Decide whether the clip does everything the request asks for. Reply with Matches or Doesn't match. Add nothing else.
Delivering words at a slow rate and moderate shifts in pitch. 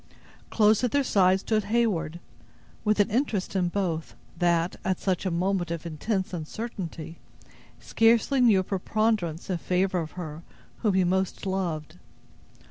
Doesn't match